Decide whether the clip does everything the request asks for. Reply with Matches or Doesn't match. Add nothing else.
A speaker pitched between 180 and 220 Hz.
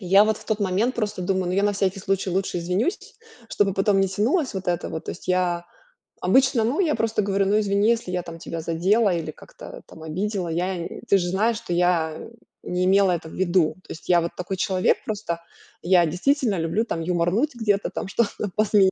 Matches